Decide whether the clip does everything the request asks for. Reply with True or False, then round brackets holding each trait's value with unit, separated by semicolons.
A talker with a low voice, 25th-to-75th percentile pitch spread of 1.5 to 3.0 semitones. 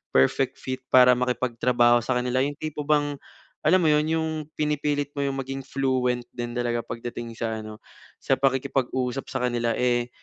True (130 Hz; 2.7 semitones)